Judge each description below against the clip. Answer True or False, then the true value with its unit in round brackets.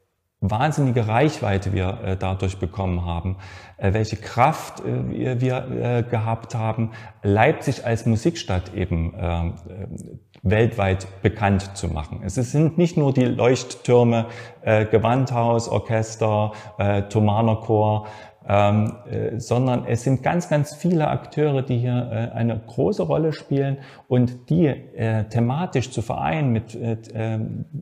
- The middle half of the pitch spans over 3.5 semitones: True (4.0 semitones)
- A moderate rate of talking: False (105 wpm)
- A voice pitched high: False (115 Hz)